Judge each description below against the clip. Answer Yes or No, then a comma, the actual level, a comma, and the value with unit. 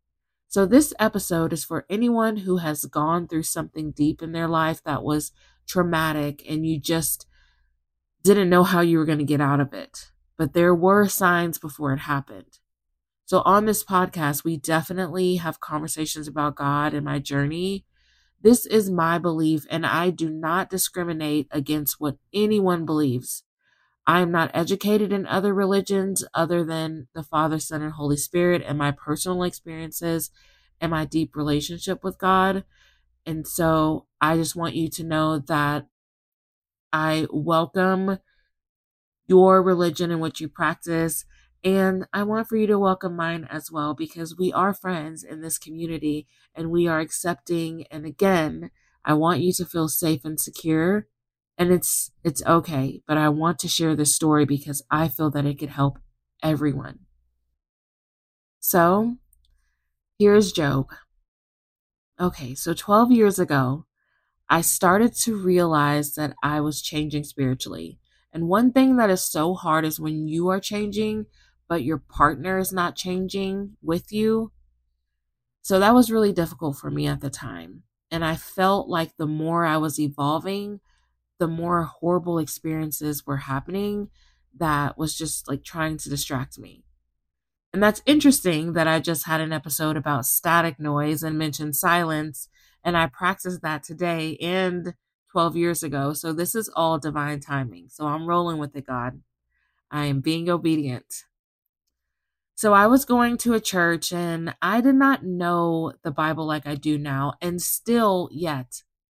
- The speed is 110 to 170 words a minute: Yes, average, 160 wpm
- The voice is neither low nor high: Yes, medium, 160 Hz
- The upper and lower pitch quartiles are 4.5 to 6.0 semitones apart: No, average, 3.3 semitones